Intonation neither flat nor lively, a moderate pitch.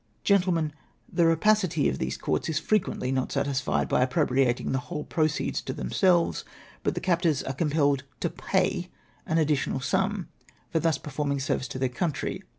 Yes: average, 4.1 semitones; medium, 150 Hz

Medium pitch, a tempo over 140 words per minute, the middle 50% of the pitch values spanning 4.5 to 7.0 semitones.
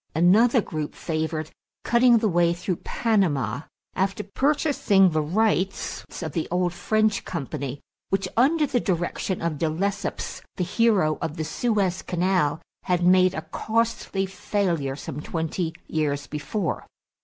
No: medium, 180 Hz; slow, 135 wpm; average, 4.8 semitones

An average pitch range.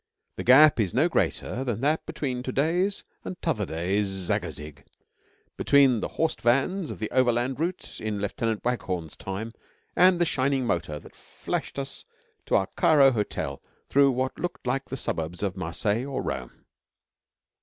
No: wide, 5.8 semitones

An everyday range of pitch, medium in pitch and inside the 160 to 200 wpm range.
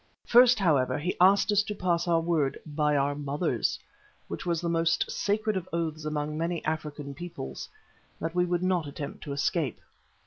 Yes: average, 3.3 semitones; medium, 165 Hz; average, 175 wpm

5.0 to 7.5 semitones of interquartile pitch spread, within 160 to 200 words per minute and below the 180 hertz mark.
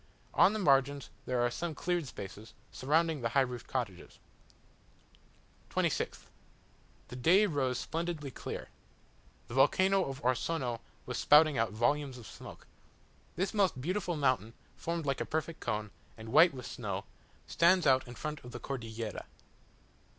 No: wide, 5.4 semitones; average, 145 wpm; low, 135 Hz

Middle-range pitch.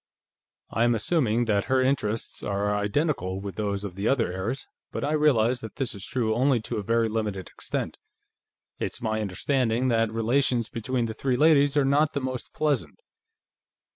No: low, 115 Hz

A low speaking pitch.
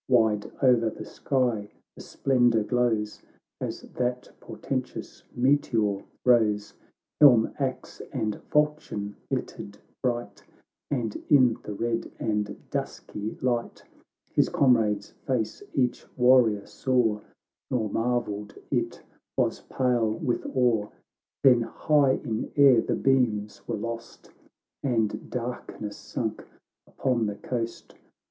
Yes: low, 120 Hz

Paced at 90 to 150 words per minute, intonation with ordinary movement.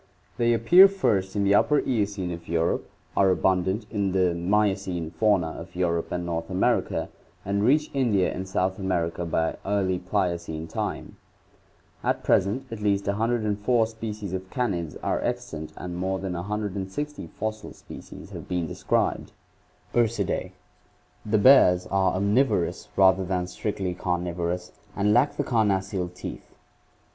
Yes: average, 140 wpm; average, 3.0 semitones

